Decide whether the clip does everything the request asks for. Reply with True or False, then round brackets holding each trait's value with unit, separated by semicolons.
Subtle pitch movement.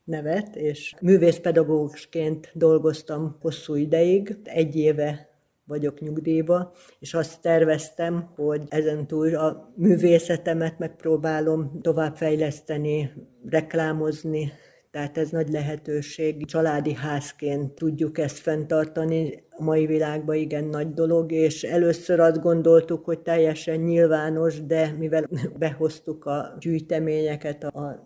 True (1.3 semitones)